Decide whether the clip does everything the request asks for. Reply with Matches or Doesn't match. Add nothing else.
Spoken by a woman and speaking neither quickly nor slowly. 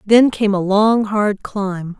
Matches